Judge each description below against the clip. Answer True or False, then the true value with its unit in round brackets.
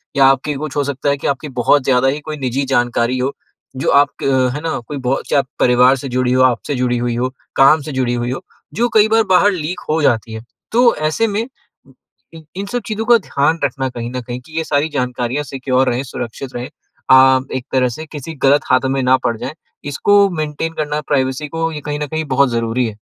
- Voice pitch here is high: False (135 Hz)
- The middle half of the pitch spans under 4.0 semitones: True (3.4 semitones)